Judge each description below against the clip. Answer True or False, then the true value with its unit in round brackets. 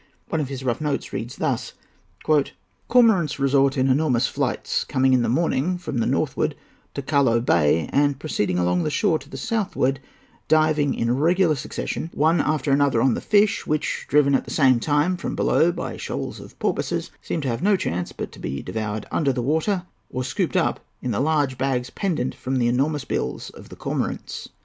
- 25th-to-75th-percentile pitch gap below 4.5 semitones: True (3.8 semitones)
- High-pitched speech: False (140 Hz)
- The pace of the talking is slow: False (185 wpm)